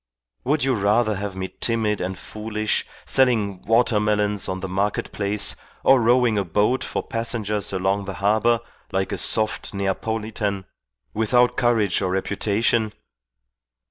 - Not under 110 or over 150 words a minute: Yes, average, 140 wpm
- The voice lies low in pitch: Yes, low, 105 Hz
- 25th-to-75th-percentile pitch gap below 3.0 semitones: Yes, narrow, 2.4 semitones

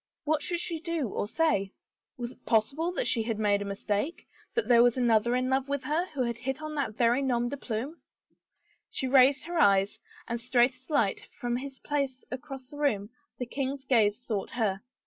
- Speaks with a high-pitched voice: Yes, very high, 255 Hz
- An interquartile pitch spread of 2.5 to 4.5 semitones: Yes, average, 3.8 semitones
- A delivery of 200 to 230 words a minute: Yes, fast, 205 wpm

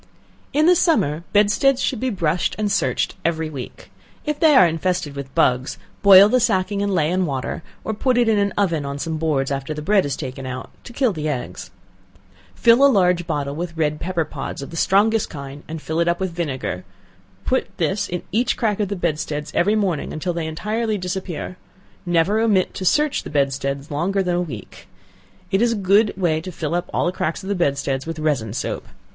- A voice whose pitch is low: No, medium, 175 Hz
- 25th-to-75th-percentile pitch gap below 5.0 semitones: No, average, 5.3 semitones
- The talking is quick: Yes, fast, 210 wpm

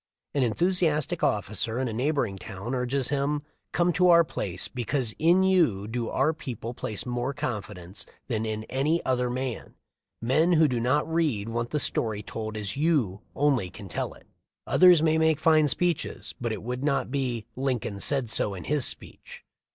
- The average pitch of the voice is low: Yes, low, 130 Hz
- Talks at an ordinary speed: Yes, average, 175 wpm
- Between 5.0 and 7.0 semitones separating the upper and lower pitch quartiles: Yes, wide, 5.5 semitones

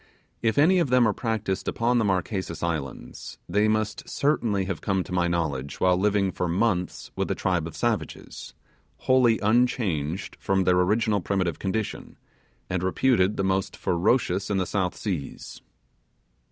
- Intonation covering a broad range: No, average, 3.7 semitones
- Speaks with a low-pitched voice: Yes, very low, 95 Hz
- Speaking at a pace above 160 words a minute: No, average, 155 wpm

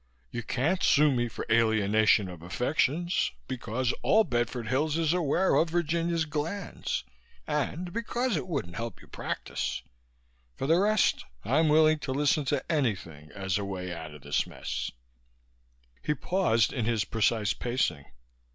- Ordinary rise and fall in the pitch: No, wide, 7.0 semitones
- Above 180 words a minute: No, average, 150 wpm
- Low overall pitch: Yes, low, 130 Hz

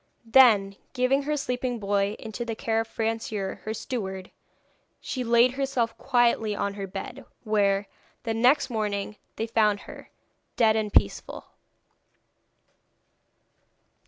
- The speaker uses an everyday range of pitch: Yes, average, 3.2 semitones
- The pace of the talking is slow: Yes, slow, 125 wpm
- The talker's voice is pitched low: No, high, 225 Hz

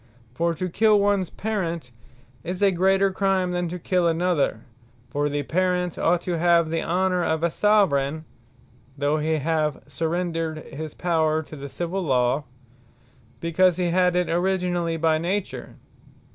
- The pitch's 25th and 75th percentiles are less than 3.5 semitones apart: Yes, narrow, 2.5 semitones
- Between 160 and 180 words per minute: No, average, 150 wpm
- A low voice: No, medium, 170 Hz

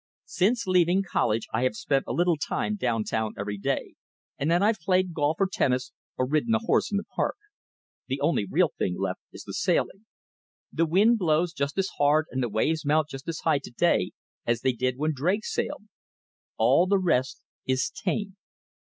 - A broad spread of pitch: Yes, wide, 6.3 semitones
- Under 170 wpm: No, average, 195 wpm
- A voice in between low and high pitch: Yes, medium, 155 Hz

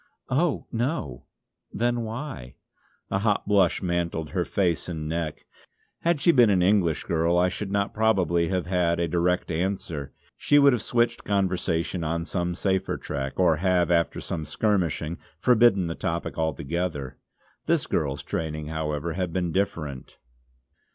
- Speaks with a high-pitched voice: No, very low, 90 Hz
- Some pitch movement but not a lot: Yes, average, 3.8 semitones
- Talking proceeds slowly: No, average, 150 wpm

